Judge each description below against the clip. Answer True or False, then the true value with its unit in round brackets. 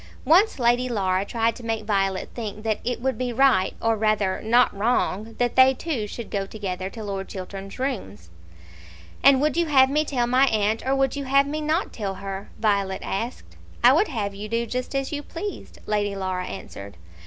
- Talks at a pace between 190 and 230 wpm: True (200 wpm)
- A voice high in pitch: True (225 Hz)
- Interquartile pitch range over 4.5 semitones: True (4.9 semitones)